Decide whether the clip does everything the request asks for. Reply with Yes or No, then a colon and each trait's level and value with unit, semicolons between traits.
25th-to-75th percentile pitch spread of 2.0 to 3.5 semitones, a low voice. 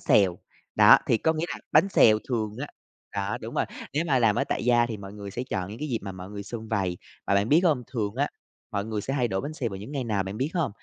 No: average, 4.9 semitones; low, 110 Hz